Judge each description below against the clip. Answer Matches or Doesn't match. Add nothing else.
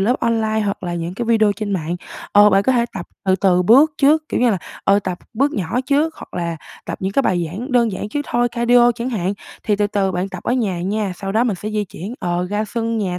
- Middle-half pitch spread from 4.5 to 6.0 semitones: Doesn't match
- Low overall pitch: Doesn't match